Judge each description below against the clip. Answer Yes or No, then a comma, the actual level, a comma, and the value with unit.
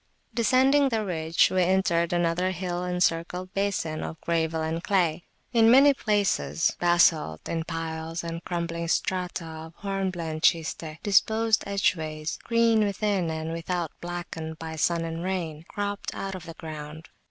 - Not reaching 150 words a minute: Yes, average, 140 wpm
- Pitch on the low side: No, medium, 175 Hz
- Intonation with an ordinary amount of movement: Yes, average, 3.2 semitones